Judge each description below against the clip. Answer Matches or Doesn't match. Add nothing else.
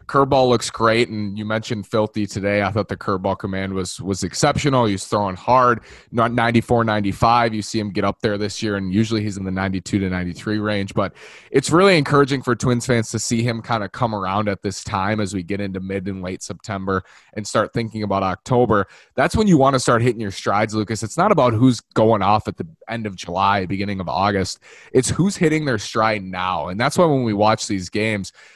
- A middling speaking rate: Doesn't match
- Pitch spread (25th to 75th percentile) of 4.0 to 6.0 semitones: Doesn't match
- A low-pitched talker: Matches